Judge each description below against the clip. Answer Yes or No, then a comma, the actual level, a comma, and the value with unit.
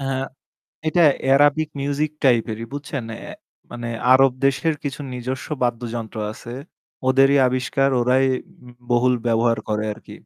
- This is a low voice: Yes, low, 130 Hz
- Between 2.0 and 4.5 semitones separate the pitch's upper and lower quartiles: Yes, narrow, 2.6 semitones